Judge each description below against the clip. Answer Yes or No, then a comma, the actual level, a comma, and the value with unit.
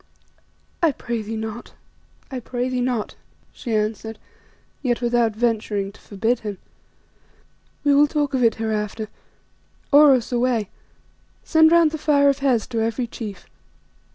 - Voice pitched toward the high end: Yes, high, 240 Hz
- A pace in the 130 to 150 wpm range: Yes, average, 140 wpm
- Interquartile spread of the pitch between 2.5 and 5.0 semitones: Yes, average, 3.8 semitones